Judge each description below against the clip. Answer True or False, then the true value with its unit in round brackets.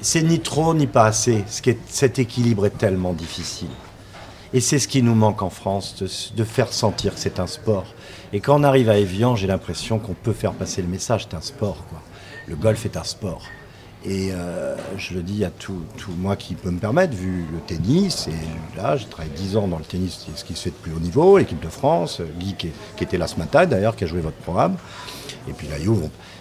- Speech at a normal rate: False (235 wpm)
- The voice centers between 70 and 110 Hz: True (100 Hz)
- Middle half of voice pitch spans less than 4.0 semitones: False (4.3 semitones)